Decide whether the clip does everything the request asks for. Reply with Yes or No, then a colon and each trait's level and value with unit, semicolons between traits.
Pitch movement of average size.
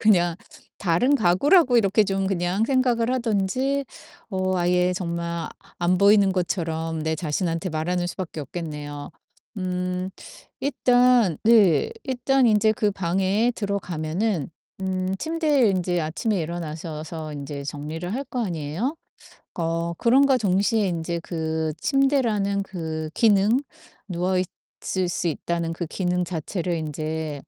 Yes: average, 4.7 semitones